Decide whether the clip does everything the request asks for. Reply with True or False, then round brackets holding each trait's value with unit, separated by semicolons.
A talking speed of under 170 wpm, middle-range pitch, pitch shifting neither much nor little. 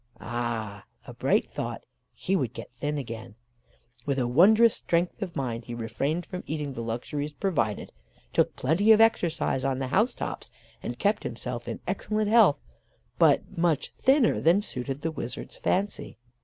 False (160 wpm; 145 Hz; 7.6 semitones)